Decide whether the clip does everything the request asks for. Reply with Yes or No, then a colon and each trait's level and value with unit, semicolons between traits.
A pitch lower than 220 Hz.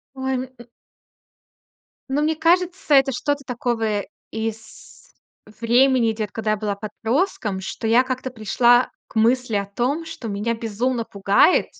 No: high, 235 Hz